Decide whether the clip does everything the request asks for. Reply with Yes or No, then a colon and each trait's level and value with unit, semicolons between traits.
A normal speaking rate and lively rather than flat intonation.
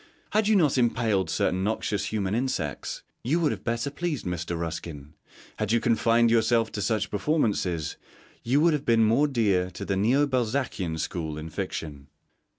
Yes: average, 165 wpm; wide, 6.0 semitones